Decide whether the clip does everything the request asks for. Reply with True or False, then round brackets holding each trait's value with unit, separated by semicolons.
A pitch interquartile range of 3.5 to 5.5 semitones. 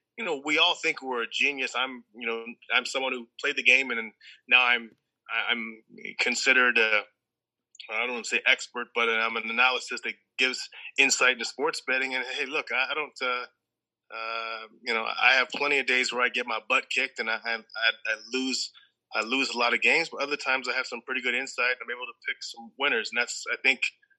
False (2.4 semitones)